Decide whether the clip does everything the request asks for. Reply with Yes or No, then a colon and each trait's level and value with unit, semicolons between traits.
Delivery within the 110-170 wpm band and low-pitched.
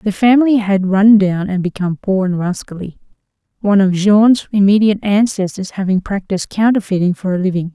No: average, 165 wpm; high, 195 Hz